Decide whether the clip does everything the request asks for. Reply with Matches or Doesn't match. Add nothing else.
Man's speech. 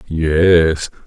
Matches